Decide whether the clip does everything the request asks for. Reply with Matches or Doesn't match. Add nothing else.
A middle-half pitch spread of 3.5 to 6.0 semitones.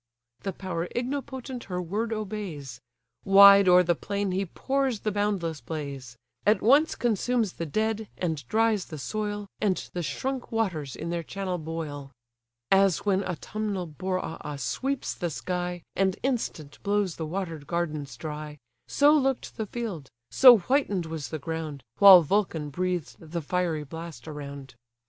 Matches